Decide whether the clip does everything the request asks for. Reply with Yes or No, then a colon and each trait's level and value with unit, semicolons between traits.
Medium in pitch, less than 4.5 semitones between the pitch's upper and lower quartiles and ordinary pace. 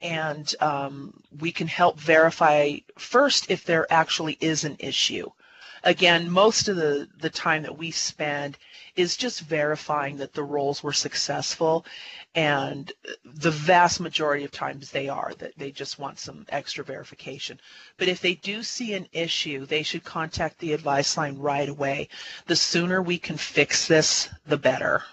Yes: medium, 160 Hz; average, 2.9 semitones; average, 160 wpm